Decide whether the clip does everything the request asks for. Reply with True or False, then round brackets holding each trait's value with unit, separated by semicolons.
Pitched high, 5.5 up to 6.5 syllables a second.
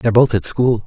False (110 Hz; 6.0 syllables/s)